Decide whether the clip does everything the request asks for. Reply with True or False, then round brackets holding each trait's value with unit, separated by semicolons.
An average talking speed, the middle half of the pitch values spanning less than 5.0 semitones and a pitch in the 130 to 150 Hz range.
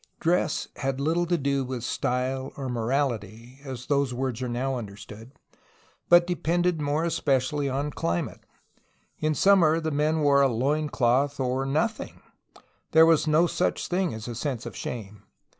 True (160 wpm; 3.9 semitones; 140 Hz)